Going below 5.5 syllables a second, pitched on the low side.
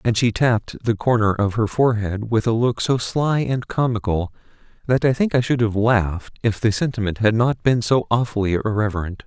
Yes: 5.3 syllables/s; low, 115 Hz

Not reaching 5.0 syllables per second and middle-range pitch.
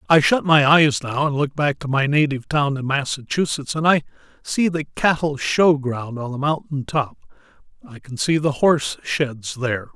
Yes: 4.8 syllables/s; medium, 145 Hz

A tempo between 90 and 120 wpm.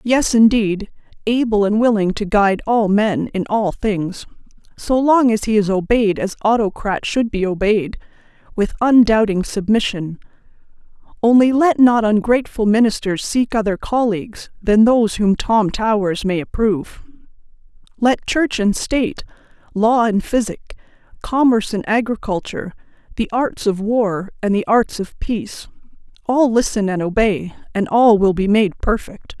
No: average, 140 wpm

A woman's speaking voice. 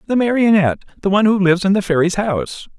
No: male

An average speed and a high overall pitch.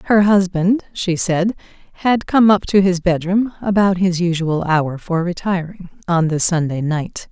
No: average, 165 wpm; medium, 180 Hz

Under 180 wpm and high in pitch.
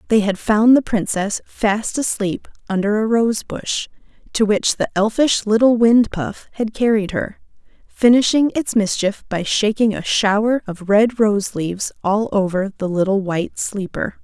Yes: average, 160 wpm; high, 210 Hz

